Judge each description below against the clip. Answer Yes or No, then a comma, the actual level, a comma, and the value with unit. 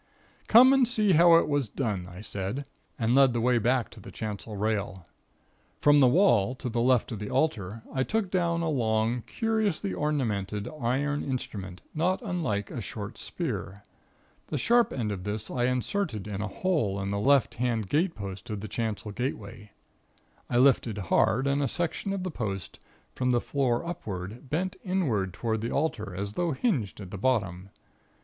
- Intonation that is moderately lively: No, wide, 6.7 semitones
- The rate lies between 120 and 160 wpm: No, average, 180 wpm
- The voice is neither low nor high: No, low, 120 Hz